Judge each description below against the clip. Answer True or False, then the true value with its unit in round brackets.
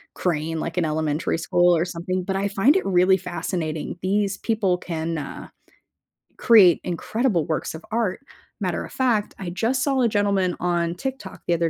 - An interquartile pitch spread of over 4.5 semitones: False (3.6 semitones)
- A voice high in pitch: False (180 Hz)